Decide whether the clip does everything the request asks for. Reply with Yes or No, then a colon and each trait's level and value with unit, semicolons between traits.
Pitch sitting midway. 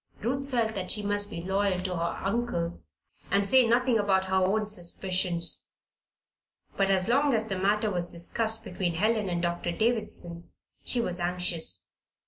No: high, 195 Hz